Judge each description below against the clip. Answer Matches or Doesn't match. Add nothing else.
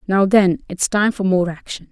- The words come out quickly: Matches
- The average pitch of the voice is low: Doesn't match